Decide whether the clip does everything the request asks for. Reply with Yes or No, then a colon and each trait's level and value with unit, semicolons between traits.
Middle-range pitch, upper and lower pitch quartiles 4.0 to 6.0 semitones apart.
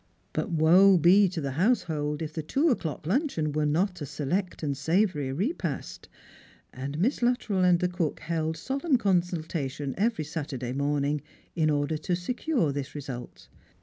Yes: medium, 160 Hz; average, 4.6 semitones